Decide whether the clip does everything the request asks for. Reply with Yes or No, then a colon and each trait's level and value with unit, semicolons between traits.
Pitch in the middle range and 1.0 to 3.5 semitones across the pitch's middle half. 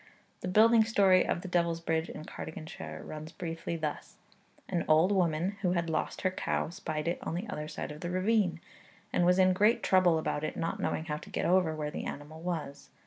Yes: medium, 170 Hz; average, 2.9 semitones